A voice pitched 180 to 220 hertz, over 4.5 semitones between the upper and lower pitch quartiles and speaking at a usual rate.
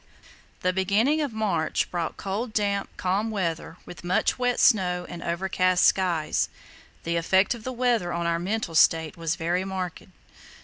No: medium, 185 Hz; average, 3.8 semitones; average, 160 wpm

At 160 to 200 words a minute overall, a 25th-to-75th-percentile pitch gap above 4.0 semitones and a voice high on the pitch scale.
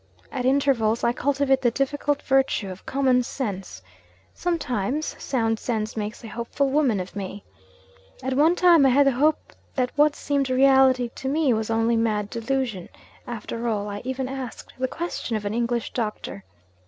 No: average, 165 wpm; average, 3.6 semitones; very high, 250 Hz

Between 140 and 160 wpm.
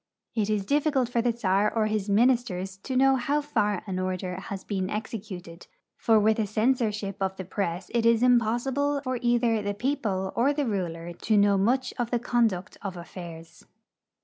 No: average, 180 wpm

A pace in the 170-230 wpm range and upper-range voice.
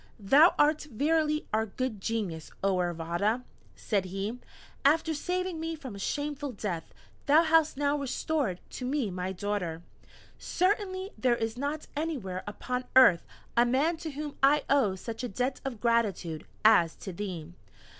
No: average, 155 wpm; very high, 250 Hz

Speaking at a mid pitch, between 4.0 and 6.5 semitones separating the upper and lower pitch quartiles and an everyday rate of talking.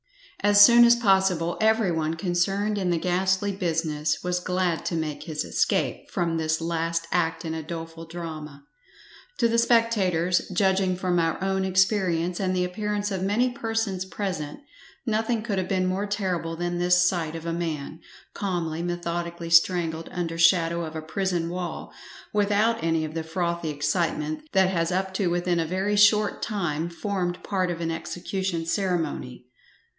No: medium, 175 Hz; average, 2.7 semitones; average, 165 wpm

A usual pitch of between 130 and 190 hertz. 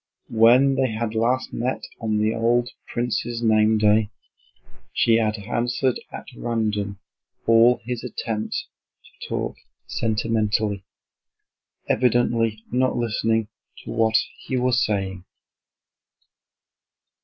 No: low, 115 Hz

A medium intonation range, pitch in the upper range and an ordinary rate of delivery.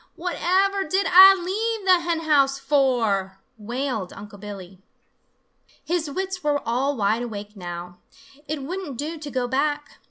No: wide, 8.5 semitones; very high, 285 Hz; average, 145 wpm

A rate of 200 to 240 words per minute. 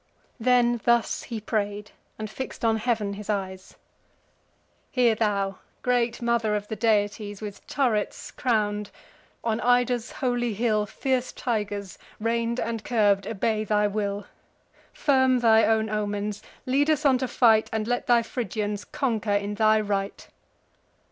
No: average, 140 wpm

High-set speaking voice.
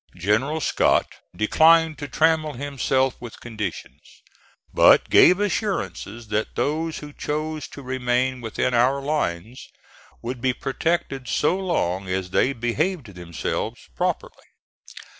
No: low, 130 Hz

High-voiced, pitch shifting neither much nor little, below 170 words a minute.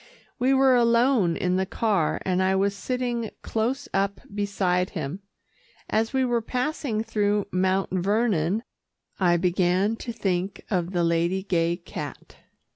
Yes: high, 200 Hz; average, 4.3 semitones; average, 140 wpm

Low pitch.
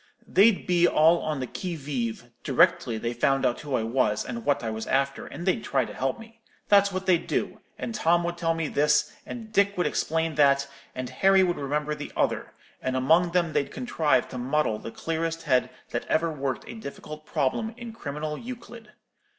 No: medium, 155 Hz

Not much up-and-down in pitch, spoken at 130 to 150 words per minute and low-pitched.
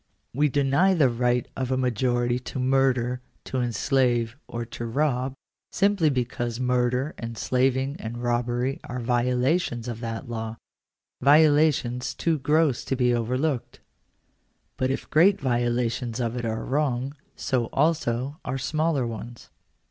Yes: narrow, 2.3 semitones; average, 140 wpm; low, 125 Hz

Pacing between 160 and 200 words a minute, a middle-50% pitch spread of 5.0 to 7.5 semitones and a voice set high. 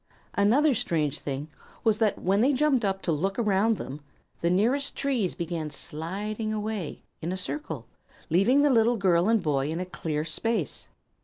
Yes: average, 170 wpm; wide, 5.4 semitones; high, 195 Hz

